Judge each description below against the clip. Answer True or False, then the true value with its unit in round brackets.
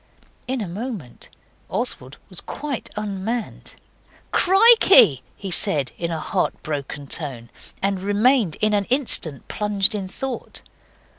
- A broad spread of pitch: True (7.4 semitones)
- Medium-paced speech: False (120 wpm)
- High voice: True (200 Hz)